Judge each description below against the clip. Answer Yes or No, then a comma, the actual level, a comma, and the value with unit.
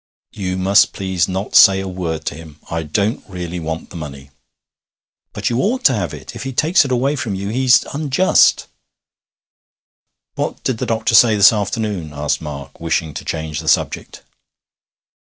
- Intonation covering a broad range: Yes, wide, 6.0 semitones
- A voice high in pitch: No, very low, 95 Hz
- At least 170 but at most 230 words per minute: Yes, average, 175 wpm